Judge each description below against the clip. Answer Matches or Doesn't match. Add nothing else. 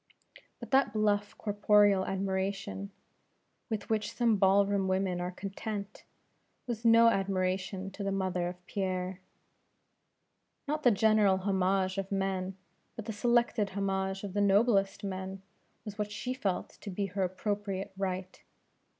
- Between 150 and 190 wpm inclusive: Doesn't match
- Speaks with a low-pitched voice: Doesn't match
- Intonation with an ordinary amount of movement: Doesn't match